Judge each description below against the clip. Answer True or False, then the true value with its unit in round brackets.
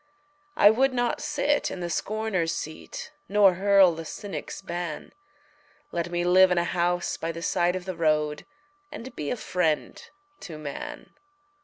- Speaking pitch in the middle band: True (180 Hz)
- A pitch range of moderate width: True (3.6 semitones)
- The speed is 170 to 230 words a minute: False (160 wpm)